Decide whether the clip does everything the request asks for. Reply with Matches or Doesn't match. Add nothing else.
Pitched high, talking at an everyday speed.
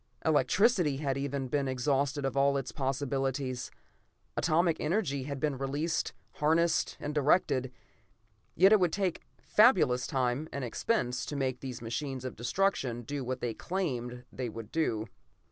Doesn't match